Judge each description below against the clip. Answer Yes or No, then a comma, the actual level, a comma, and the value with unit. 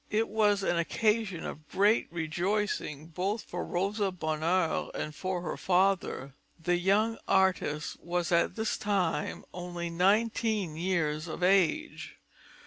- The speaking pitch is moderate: Yes, medium, 180 Hz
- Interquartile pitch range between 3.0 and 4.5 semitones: Yes, average, 3.5 semitones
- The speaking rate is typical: No, slow, 130 wpm